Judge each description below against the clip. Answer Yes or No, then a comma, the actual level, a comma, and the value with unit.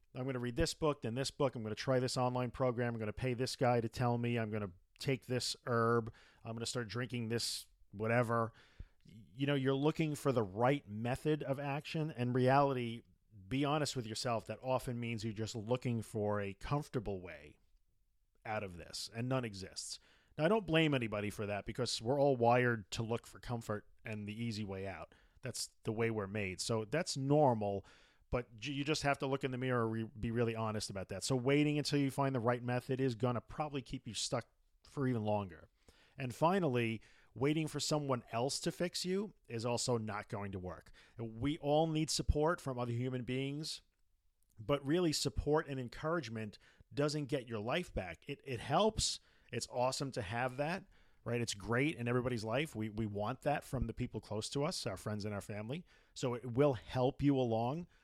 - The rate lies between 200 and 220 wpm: Yes, fast, 205 wpm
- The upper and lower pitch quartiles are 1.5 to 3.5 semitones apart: No, average, 4.1 semitones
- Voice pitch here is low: Yes, low, 125 Hz